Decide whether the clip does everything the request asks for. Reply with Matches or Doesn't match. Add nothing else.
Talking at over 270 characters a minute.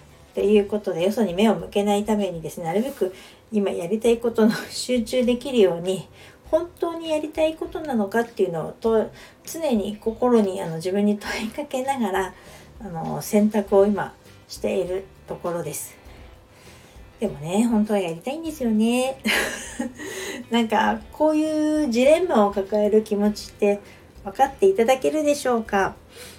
Matches